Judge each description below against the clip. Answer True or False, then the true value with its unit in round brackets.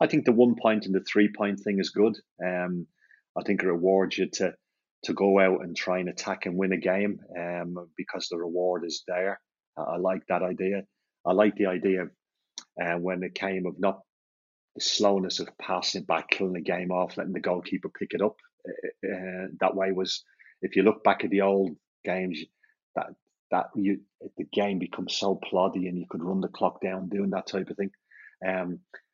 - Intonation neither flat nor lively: False (1.4 semitones)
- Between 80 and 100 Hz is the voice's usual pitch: True (95 Hz)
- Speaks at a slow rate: False (205 wpm)